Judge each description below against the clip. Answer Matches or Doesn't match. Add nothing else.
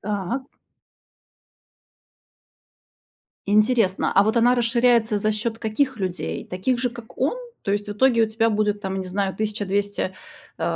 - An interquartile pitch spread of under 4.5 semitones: Matches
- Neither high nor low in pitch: Doesn't match